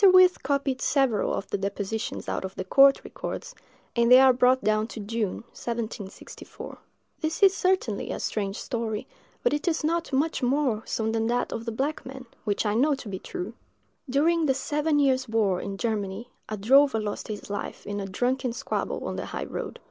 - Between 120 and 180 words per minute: No, average, 195 wpm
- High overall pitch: Yes, high, 240 Hz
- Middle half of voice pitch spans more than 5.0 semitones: No, average, 4.7 semitones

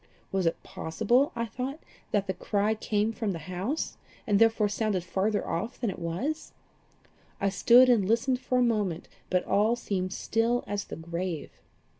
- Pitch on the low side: No, high, 210 Hz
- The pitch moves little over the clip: No, average, 3.9 semitones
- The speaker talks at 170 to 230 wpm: Yes, average, 175 wpm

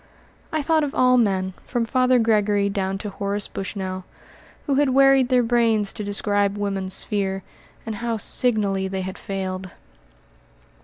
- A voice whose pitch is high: Yes, high, 205 Hz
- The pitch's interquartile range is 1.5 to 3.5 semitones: No, average, 3.9 semitones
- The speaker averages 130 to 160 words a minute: Yes, average, 150 wpm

